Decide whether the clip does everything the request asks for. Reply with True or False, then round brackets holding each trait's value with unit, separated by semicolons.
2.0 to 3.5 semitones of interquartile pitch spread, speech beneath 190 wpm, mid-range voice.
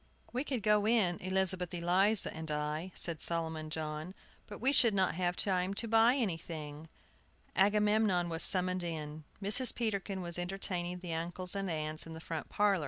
False (3.9 semitones; 170 wpm; 180 Hz)